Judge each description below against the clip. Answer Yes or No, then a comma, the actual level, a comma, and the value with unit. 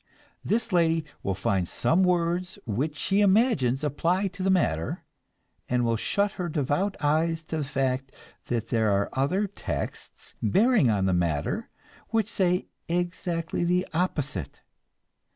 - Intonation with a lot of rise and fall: Yes, wide, 6.8 semitones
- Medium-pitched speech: Yes, medium, 165 Hz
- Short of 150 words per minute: Yes, average, 140 wpm